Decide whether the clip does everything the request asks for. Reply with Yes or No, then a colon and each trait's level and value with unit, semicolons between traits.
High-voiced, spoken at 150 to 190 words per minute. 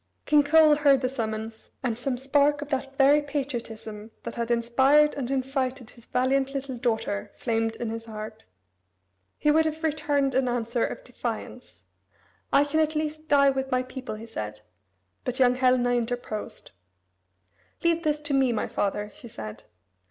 Yes: very high, 260 Hz; average, 165 wpm